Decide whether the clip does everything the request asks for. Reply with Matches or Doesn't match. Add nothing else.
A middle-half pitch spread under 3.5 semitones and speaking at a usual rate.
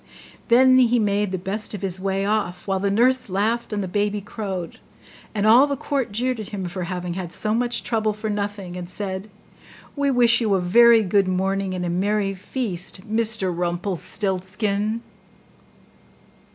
Matches